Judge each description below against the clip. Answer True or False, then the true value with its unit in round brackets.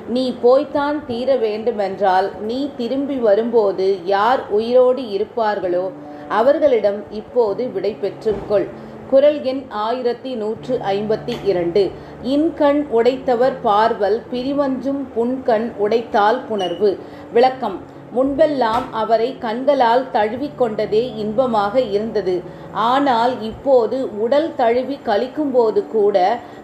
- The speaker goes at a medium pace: True (90 wpm)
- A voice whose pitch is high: True (230 Hz)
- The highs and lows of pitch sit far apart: False (3.8 semitones)